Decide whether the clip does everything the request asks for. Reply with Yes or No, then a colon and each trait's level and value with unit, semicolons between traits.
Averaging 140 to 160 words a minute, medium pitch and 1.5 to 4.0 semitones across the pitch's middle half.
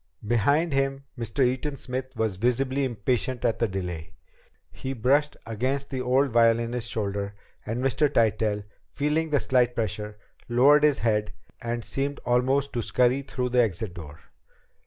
No: average, 150 wpm; low, 125 Hz; average, 3.6 semitones